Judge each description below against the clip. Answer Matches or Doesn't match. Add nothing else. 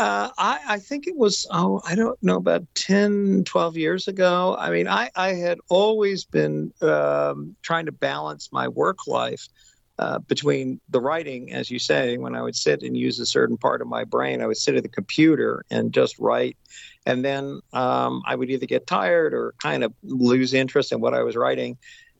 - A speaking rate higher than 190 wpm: Matches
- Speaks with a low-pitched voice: Matches